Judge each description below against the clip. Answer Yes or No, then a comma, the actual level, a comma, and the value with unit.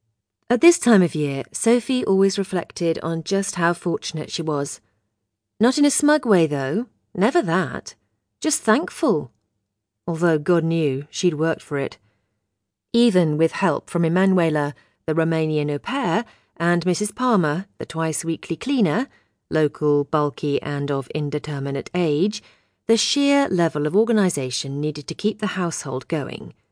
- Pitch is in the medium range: Yes, medium, 165 Hz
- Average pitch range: No, wide, 5.9 semitones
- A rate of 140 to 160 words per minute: Yes, average, 145 wpm